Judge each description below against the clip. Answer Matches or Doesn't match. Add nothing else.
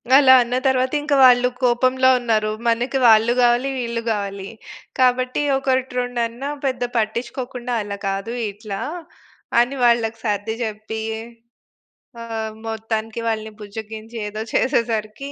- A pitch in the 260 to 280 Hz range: Doesn't match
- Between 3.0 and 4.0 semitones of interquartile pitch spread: Doesn't match